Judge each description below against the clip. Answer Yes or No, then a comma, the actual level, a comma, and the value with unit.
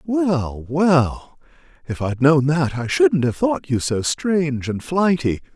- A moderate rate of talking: Yes, average, 160 wpm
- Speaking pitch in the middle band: Yes, medium, 145 Hz